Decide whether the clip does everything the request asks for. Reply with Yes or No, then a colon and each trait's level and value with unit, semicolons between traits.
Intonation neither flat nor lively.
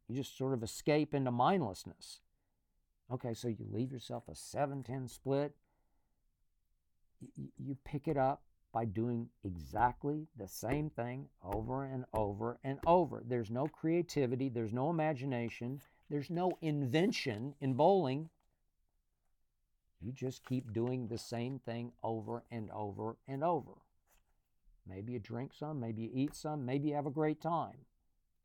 Yes: average, 4.2 semitones